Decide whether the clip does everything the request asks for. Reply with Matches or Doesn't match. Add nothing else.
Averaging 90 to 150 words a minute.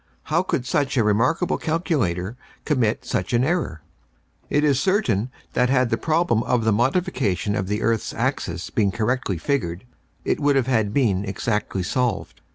Doesn't match